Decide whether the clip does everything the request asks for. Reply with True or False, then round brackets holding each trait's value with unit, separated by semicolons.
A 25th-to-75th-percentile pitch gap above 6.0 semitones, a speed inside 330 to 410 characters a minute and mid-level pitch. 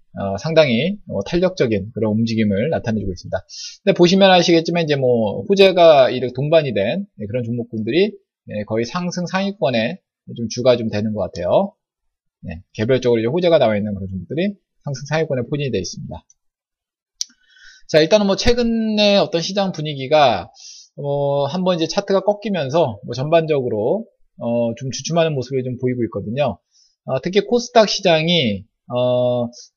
True (8.1 semitones; 345 characters per minute; 145 Hz)